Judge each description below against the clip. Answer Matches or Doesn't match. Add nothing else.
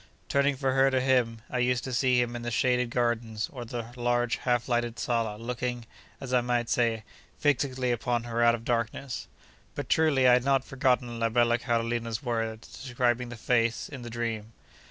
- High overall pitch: Doesn't match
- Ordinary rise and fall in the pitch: Doesn't match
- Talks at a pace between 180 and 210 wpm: Matches